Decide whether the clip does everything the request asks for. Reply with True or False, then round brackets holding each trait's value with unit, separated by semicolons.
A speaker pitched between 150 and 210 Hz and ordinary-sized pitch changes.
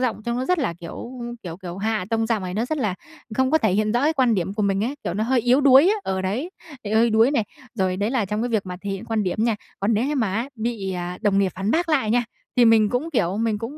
False (220 Hz; 4.0 semitones)